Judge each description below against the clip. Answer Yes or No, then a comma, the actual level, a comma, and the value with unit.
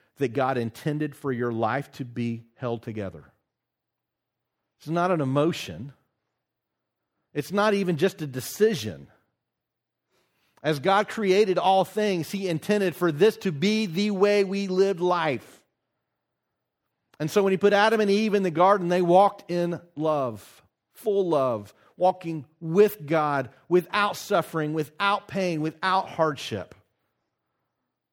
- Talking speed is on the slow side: Yes, slow, 130 wpm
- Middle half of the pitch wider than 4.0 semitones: Yes, wide, 5.4 semitones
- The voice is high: No, medium, 175 Hz